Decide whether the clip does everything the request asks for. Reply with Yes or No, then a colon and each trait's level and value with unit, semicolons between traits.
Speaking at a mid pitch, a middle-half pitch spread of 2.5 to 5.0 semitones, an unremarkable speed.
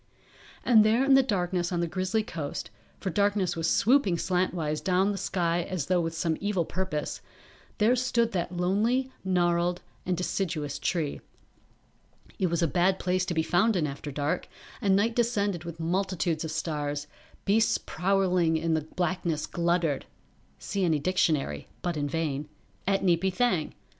Yes: medium, 180 Hz; average, 3.2 semitones; average, 160 wpm